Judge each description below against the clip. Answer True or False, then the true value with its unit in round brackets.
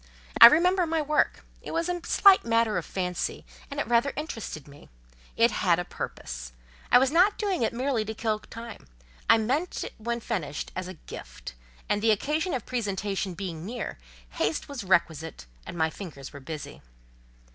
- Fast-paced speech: False (180 wpm)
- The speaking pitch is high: True (220 Hz)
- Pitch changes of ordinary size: False (8.4 semitones)